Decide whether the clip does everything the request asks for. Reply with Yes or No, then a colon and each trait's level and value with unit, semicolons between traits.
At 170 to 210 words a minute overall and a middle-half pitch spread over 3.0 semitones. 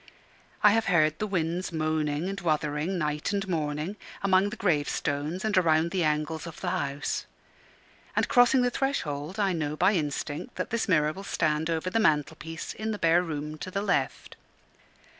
Yes: average, 175 wpm; average, 4.4 semitones